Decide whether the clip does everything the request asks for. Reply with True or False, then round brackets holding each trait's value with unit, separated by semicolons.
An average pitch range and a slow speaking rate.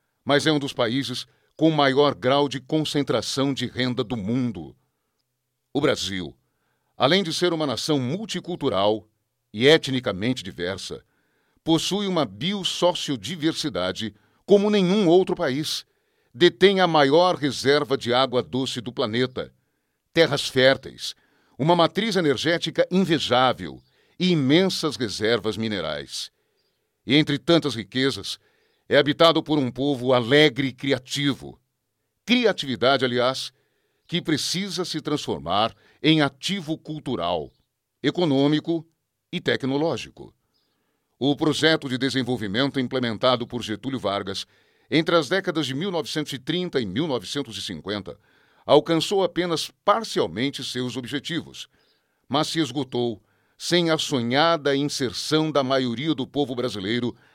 True (4.4 semitones; 110 wpm)